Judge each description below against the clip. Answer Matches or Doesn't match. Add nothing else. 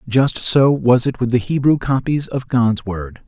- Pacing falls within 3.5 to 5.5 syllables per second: Matches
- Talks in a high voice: Doesn't match